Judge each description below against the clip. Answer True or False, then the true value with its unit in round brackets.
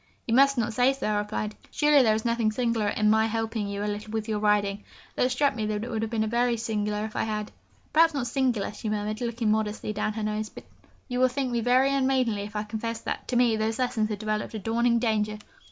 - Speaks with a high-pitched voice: True (220 Hz)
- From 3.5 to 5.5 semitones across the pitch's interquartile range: False (2.4 semitones)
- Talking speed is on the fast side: True (250 wpm)